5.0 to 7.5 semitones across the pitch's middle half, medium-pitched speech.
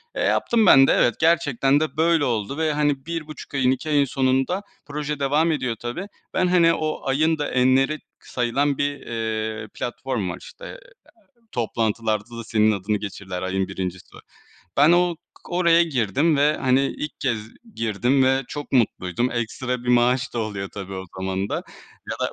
No: average, 5.3 semitones; low, 130 Hz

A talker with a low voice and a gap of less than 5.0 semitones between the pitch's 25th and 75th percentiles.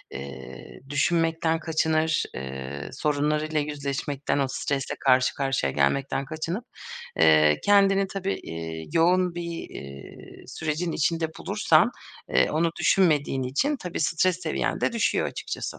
No: medium, 150 Hz; average, 4.6 semitones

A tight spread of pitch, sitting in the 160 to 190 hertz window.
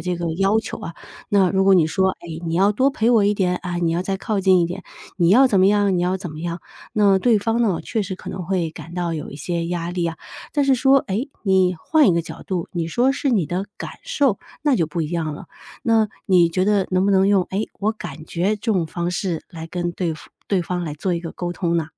No: average, 3.1 semitones; medium, 185 Hz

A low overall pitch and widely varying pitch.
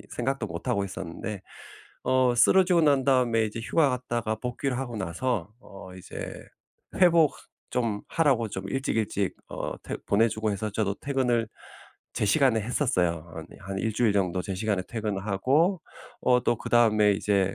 No: low, 110 Hz; average, 4.5 semitones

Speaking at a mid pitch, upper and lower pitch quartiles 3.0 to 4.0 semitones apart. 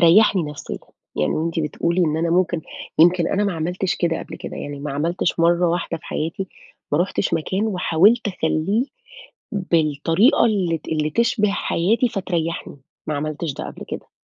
Yes: medium, 170 Hz; average, 3.3 semitones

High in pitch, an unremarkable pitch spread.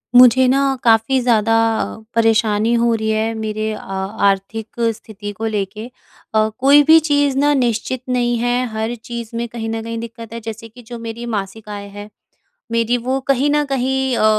No: high, 230 Hz; narrow, 2.3 semitones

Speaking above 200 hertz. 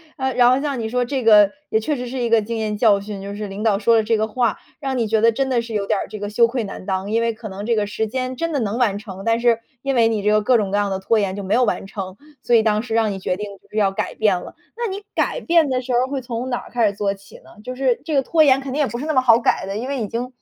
Yes: high, 230 Hz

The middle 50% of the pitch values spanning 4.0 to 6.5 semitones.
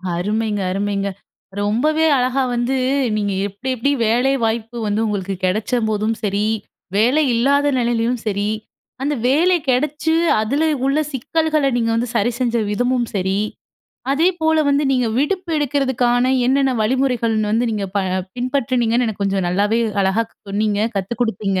Yes: average, 4.5 semitones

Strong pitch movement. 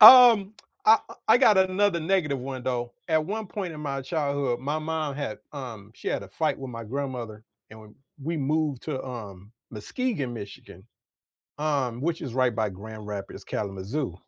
Yes: wide, 5.7 semitones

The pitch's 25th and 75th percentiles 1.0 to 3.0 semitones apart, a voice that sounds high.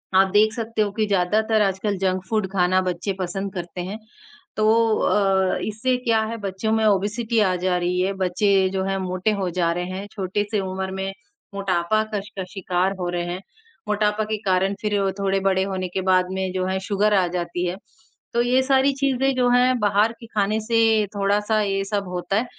Yes: narrow, 2.6 semitones; high, 195 Hz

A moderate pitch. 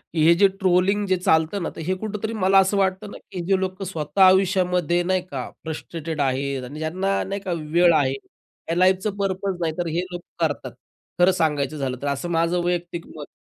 Yes: medium, 175 Hz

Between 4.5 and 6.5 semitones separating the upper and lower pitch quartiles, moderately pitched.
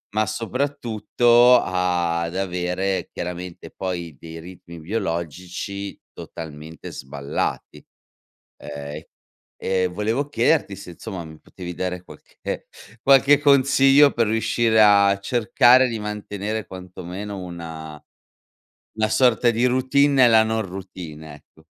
No: average, 5.0 semitones; very low, 95 Hz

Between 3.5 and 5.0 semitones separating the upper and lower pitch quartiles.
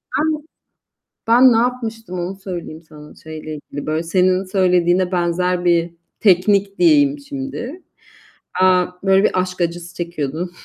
Yes: average, 4.6 semitones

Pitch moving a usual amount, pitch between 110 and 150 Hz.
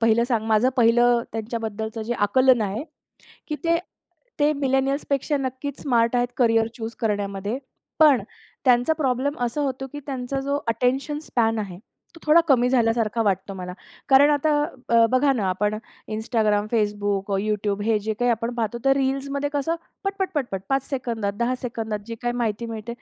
No: average, 3.6 semitones; high, 240 Hz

